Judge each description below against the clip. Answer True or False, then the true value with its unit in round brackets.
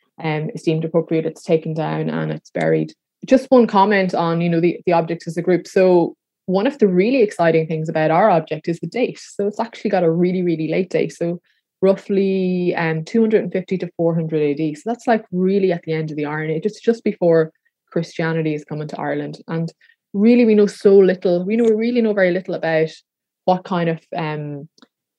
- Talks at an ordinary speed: False (220 wpm)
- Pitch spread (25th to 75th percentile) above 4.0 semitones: False (3.7 semitones)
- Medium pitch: True (175 Hz)